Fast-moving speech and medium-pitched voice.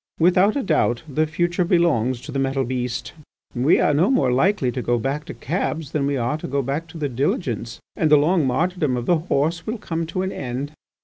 Yes: fast, 225 wpm; medium, 150 Hz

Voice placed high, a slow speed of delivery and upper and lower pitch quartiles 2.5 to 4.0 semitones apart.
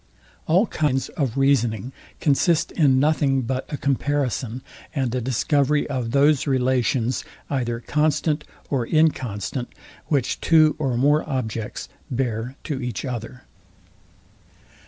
No: low, 135 Hz; slow, 115 wpm; average, 3.1 semitones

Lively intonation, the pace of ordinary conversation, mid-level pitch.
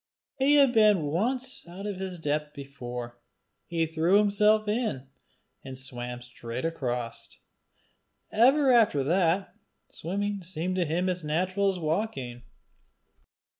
No: wide, 6.6 semitones; slow, 125 wpm; medium, 175 Hz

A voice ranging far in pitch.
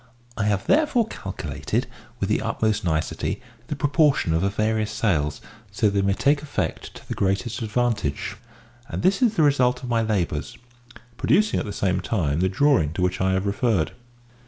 Yes: wide, 6.0 semitones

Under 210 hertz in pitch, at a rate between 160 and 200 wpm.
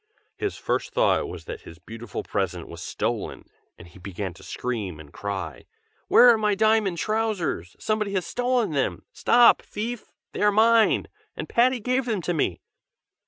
Yes: high, 190 Hz; average, 165 wpm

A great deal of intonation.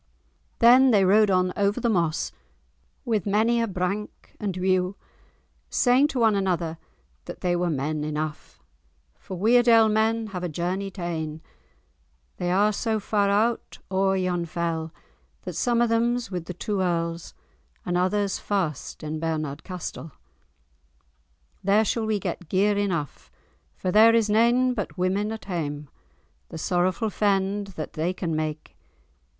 No: average, 4.0 semitones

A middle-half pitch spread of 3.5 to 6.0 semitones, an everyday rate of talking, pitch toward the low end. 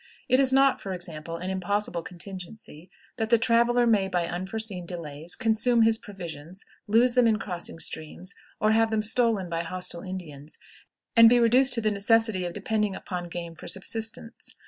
No: average, 4.4 semitones; average, 170 wpm; high, 200 Hz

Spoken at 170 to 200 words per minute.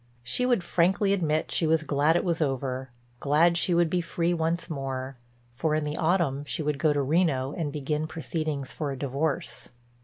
Yes: average, 190 wpm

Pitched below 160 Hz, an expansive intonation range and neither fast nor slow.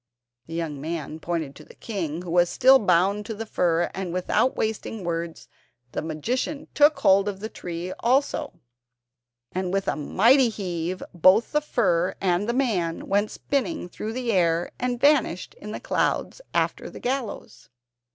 No: high, 190 Hz; wide, 5.8 semitones; average, 160 wpm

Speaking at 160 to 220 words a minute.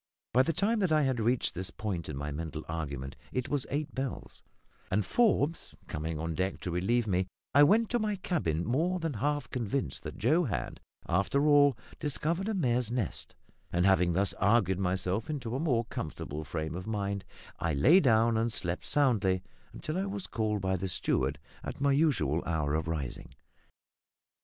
Yes: average, 180 wpm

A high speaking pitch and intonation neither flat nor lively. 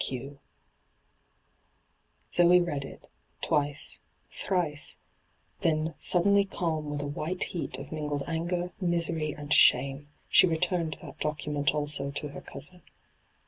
No: medium, 155 Hz; average, 3.1 semitones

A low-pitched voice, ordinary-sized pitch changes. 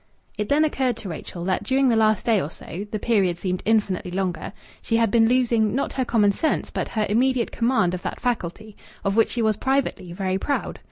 No: high, 215 Hz; average, 4.2 semitones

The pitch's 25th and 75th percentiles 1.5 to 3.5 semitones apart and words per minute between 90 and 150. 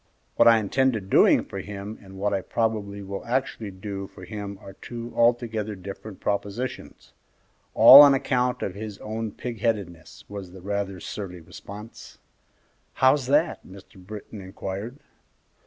Yes: average, 3.1 semitones; average, 145 wpm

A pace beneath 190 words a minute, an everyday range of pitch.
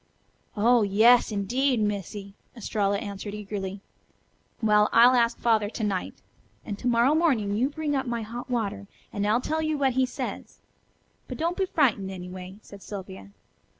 Yes: average, 160 wpm; average, 3.8 semitones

